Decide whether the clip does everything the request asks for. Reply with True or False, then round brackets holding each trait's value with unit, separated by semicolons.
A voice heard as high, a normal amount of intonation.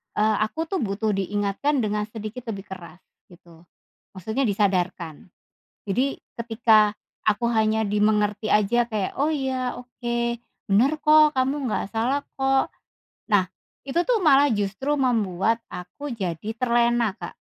True (220 Hz; 4.2 semitones)